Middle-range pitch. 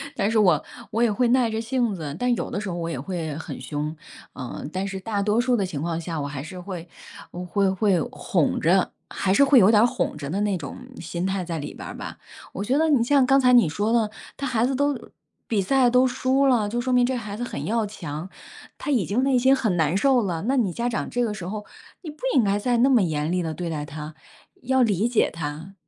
No: high, 205 Hz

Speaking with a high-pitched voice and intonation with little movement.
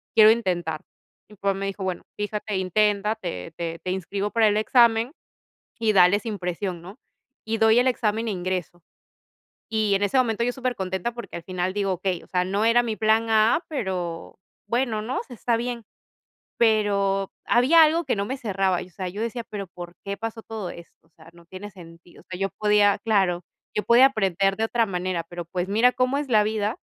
No: high, 205 Hz; average, 3.4 semitones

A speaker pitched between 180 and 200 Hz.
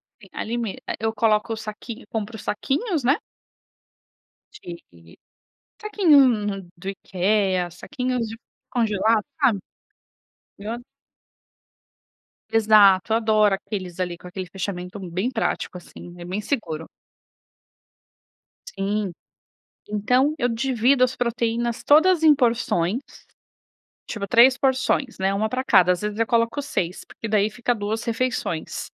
No: high, 220 Hz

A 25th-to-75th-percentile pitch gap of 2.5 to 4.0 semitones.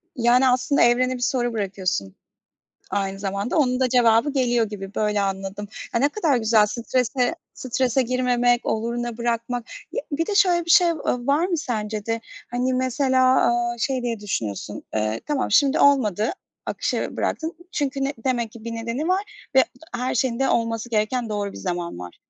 Yes: average, 3.4 semitones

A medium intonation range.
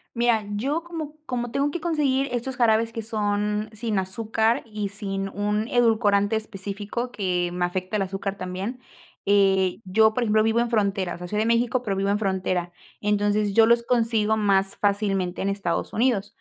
Yes: average, 3.0 semitones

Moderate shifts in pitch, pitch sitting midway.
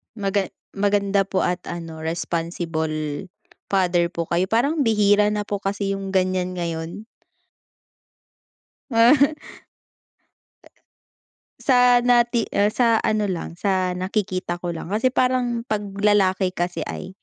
No: average, 3.6 semitones; high, 195 Hz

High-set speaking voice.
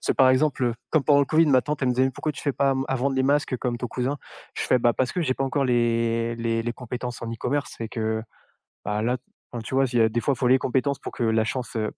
No: low, 125 Hz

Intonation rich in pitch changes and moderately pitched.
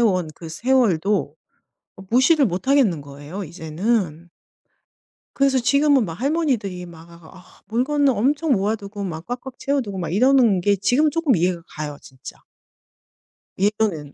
No: wide, 7.3 semitones; high, 205 Hz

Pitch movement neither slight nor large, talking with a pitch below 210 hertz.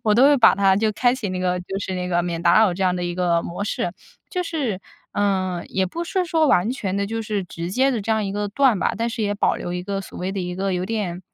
Yes: average, 3.8 semitones; high, 195 Hz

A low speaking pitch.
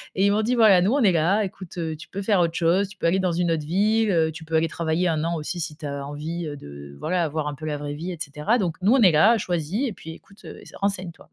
No: medium, 170 Hz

